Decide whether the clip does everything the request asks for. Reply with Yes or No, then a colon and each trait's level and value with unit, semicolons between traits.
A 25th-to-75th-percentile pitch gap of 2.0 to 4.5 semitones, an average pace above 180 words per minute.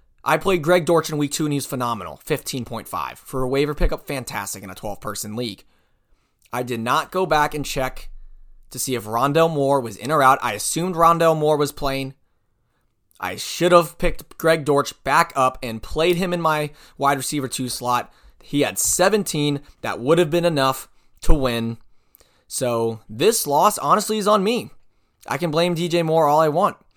No: average, 5.2 semitones; average, 190 wpm